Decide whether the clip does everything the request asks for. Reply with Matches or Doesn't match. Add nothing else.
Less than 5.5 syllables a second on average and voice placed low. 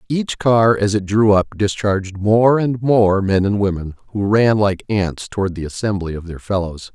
Matches